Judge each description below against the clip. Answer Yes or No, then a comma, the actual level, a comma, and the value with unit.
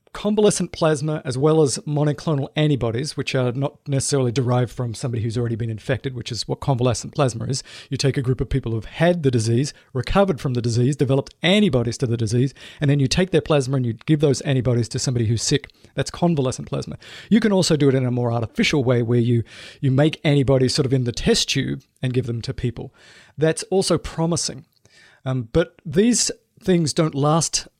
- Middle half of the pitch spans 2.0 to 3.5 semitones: No, average, 3.9 semitones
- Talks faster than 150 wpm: Yes, fast, 205 wpm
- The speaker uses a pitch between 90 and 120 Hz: No, low, 135 Hz